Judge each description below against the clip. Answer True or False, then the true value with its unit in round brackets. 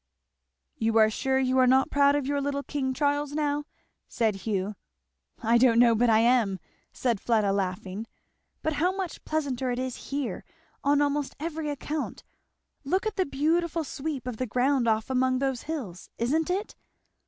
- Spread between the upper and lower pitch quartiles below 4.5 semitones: True (4.0 semitones)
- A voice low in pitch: False (265 Hz)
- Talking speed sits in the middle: True (170 wpm)